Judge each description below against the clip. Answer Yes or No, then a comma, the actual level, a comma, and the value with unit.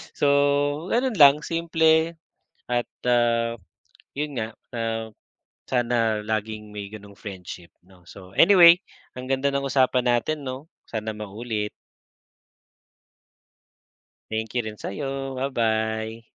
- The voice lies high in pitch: No, low, 115 Hz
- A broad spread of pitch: No, average, 4.1 semitones